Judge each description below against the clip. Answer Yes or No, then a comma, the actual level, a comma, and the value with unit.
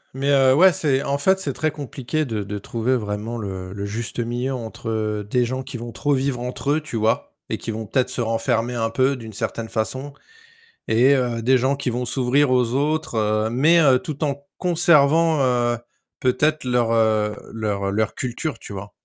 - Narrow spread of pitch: No, average, 3.8 semitones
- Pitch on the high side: No, low, 125 Hz